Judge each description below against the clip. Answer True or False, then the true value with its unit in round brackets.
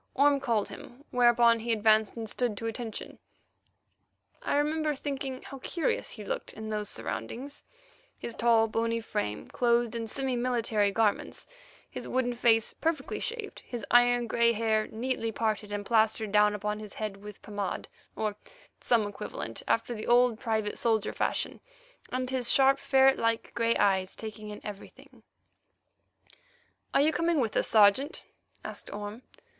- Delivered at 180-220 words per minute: False (150 wpm)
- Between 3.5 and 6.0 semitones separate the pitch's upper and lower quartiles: False (3.1 semitones)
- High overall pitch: True (230 Hz)